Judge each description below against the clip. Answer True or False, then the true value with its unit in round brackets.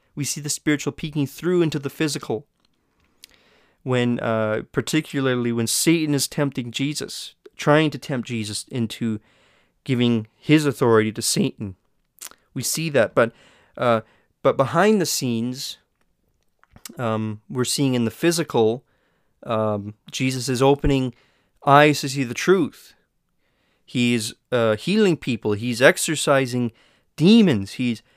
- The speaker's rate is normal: False (130 wpm)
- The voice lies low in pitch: True (130 Hz)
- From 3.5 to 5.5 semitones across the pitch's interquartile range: True (4.2 semitones)